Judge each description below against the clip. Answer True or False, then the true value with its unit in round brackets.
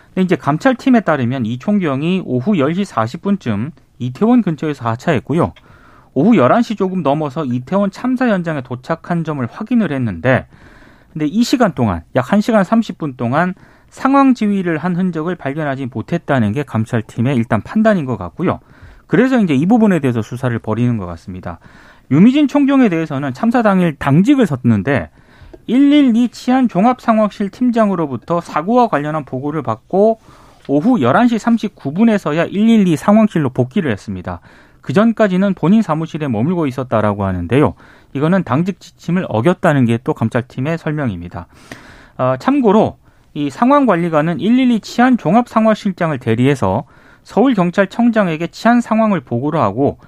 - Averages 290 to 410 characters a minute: True (325 characters per minute)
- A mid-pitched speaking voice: True (165 Hz)